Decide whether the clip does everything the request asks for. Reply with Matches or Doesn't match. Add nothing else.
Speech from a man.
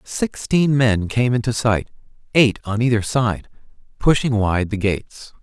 Matches